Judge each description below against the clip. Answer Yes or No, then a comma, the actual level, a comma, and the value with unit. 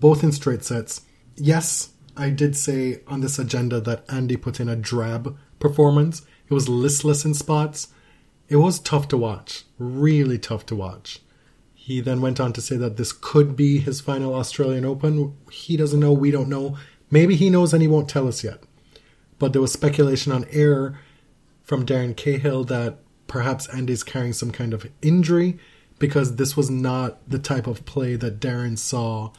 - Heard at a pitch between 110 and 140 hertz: Yes, low, 135 Hz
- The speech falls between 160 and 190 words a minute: Yes, average, 180 wpm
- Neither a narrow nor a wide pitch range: Yes, average, 3.0 semitones